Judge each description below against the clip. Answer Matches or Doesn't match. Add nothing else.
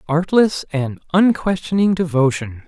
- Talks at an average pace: Doesn't match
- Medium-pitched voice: Matches